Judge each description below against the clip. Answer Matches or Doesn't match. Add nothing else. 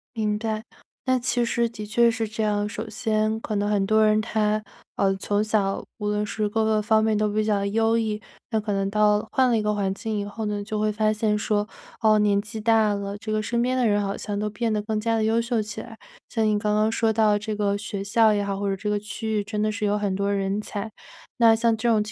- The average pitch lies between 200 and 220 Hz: Matches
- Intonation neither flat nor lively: Doesn't match